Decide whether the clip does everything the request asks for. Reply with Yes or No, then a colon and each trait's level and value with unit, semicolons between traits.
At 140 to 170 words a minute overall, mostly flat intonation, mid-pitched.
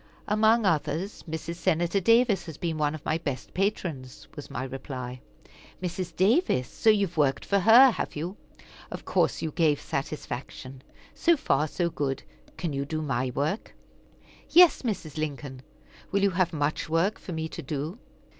No: average, 165 wpm; average, 5.3 semitones; medium, 160 Hz